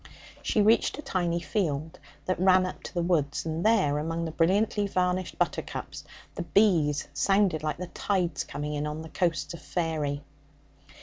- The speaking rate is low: No, average, 170 wpm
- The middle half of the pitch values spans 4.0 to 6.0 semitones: No, average, 3.4 semitones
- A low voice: No, medium, 170 Hz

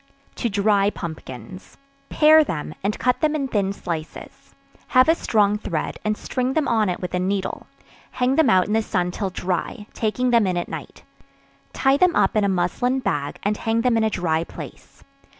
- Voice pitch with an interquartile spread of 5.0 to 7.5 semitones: Yes, wide, 5.6 semitones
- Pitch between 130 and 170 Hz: No, high, 210 Hz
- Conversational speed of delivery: Yes, average, 195 wpm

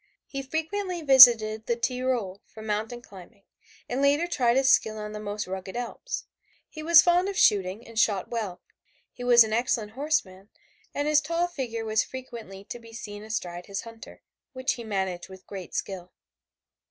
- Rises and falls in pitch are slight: No, average, 4.4 semitones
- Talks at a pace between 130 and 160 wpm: No, average, 175 wpm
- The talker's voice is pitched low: No, high, 230 Hz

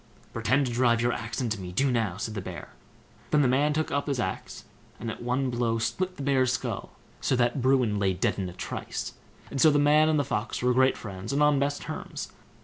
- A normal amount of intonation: Yes, average, 3.7 semitones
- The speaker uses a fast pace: Yes, fast, 235 wpm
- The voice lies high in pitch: No, low, 125 Hz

